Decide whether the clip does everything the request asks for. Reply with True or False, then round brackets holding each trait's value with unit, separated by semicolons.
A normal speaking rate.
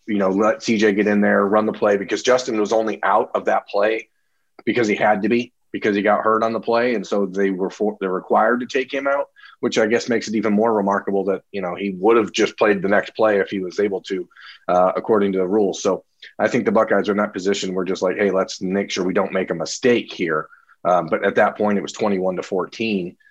False (265 wpm)